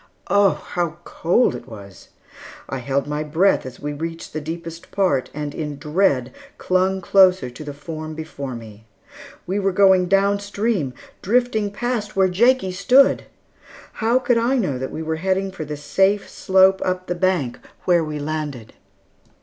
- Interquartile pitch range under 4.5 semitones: No, average, 4.9 semitones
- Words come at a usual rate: Yes, average, 165 wpm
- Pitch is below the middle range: No, medium, 175 Hz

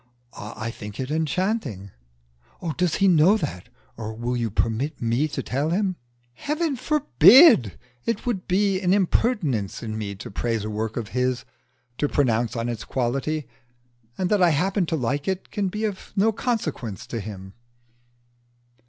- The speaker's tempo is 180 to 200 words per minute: No, average, 160 wpm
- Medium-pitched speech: Yes, medium, 145 Hz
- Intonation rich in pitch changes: Yes, wide, 9.0 semitones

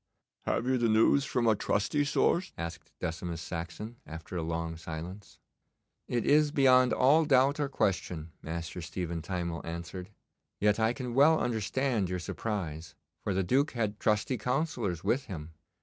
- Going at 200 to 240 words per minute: No, average, 155 wpm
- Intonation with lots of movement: Yes, wide, 7.1 semitones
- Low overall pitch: Yes, low, 105 Hz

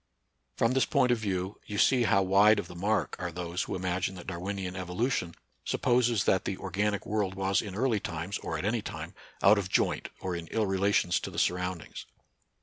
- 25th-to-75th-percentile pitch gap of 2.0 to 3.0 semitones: Yes, narrow, 2.6 semitones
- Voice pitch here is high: No, very low, 95 Hz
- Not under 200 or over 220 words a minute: Yes, fast, 205 wpm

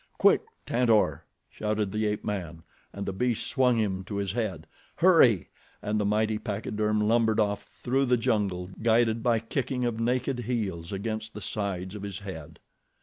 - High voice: No, low, 105 Hz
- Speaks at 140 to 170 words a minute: Yes, average, 165 wpm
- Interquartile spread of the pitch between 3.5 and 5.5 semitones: No, average, 2.8 semitones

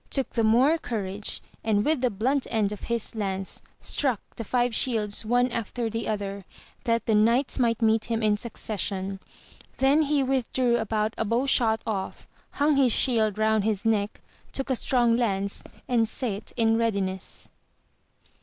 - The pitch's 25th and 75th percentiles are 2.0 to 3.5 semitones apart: Yes, average, 2.8 semitones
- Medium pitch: No, high, 225 Hz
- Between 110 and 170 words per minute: Yes, average, 165 wpm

